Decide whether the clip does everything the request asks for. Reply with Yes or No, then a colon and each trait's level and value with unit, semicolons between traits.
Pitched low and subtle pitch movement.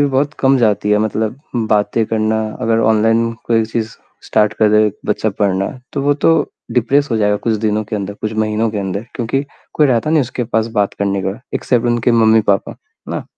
Yes: low, 110 Hz; narrow, 2.2 semitones